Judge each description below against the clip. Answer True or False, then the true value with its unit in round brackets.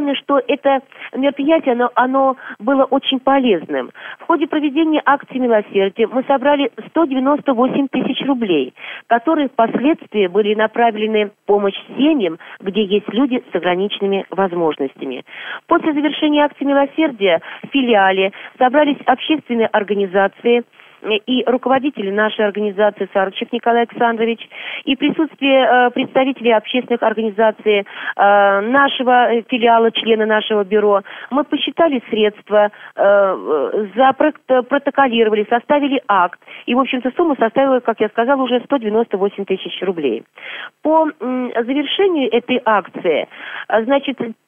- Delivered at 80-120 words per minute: True (115 wpm)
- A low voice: False (245 Hz)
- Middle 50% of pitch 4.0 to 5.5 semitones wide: True (4.7 semitones)